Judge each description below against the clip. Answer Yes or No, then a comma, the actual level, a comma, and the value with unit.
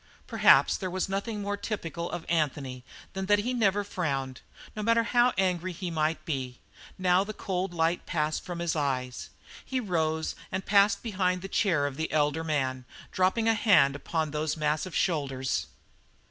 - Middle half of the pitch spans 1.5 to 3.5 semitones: No, average, 4.6 semitones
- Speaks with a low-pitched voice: No, medium, 175 Hz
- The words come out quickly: No, average, 170 wpm